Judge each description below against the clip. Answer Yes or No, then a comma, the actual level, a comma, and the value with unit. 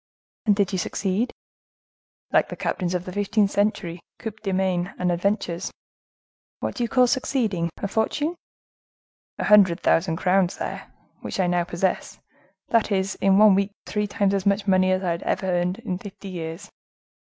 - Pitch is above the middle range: Yes, high, 195 Hz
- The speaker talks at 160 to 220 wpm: Yes, average, 165 wpm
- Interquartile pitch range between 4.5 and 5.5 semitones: No, narrow, 2.4 semitones